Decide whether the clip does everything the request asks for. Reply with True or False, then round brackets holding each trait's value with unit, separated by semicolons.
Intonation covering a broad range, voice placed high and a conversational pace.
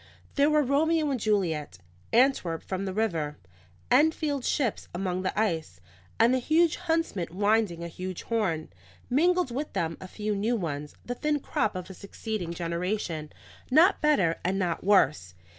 True (8.1 semitones; 205 Hz; 160 wpm)